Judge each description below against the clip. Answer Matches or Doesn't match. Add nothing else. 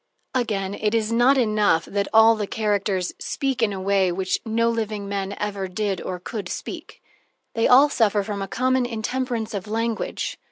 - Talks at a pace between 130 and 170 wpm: Doesn't match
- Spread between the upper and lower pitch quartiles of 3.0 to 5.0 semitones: Doesn't match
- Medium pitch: Doesn't match